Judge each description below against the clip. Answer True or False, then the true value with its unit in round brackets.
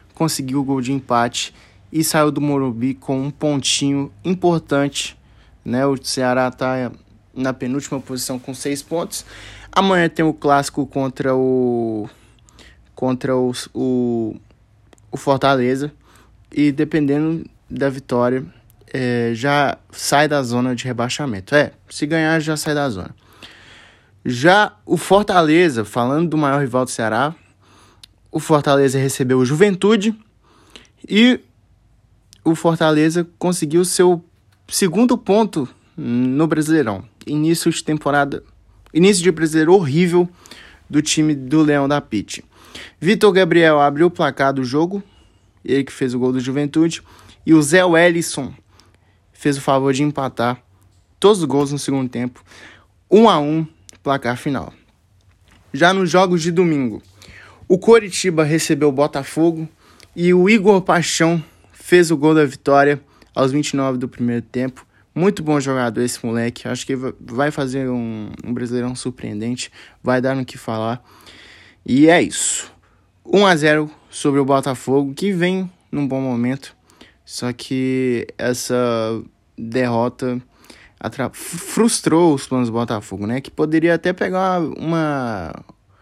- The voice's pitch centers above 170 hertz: False (135 Hz)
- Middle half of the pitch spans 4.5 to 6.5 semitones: True (4.9 semitones)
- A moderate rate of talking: True (135 wpm)